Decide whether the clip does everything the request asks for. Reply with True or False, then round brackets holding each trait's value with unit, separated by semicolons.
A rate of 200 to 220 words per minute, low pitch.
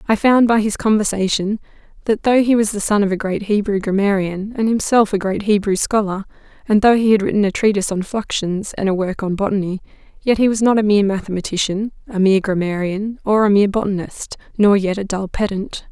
False (205 wpm; 205 Hz)